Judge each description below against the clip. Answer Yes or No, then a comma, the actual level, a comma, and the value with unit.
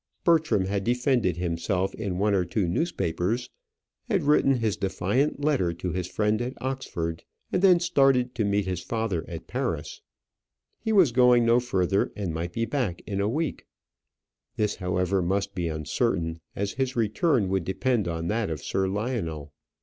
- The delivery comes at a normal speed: Yes, average, 165 wpm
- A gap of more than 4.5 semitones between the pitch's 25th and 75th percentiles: Yes, wide, 5.6 semitones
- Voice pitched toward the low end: Yes, low, 105 Hz